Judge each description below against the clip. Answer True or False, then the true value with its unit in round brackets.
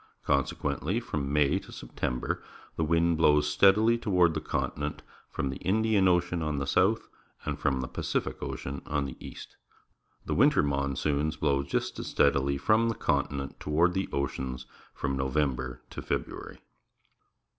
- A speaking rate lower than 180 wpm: True (150 wpm)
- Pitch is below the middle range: True (75 Hz)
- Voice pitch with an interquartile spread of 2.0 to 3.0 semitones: False (3.7 semitones)